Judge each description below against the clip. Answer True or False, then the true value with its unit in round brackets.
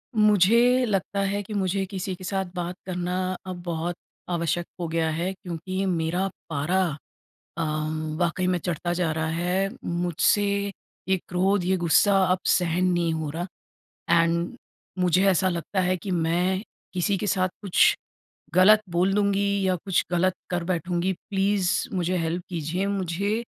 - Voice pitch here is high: False (180 Hz)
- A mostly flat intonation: True (2.0 semitones)